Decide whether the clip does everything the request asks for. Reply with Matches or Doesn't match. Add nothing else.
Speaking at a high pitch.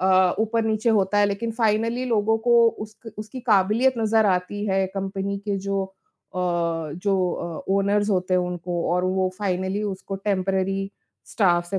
Matches